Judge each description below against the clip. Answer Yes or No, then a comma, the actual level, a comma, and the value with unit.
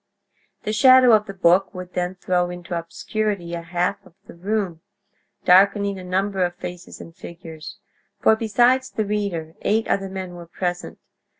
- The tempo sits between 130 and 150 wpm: No, average, 165 wpm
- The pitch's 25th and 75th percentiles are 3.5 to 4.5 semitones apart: No, average, 2.9 semitones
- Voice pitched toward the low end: No, medium, 185 Hz